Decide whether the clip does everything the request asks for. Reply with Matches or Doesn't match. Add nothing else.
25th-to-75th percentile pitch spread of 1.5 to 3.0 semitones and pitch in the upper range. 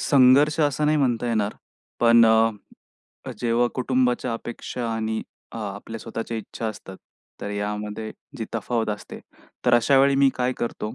Doesn't match